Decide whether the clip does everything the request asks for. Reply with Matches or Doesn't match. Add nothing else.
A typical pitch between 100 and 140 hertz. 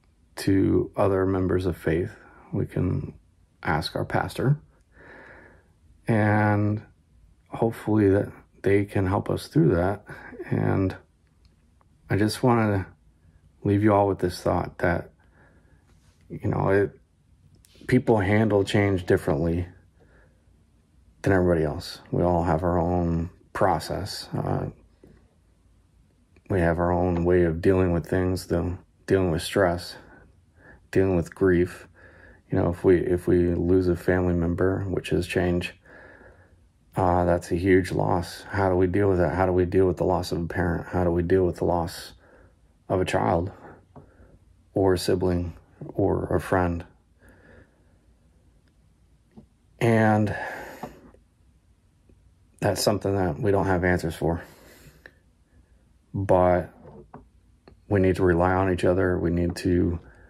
Doesn't match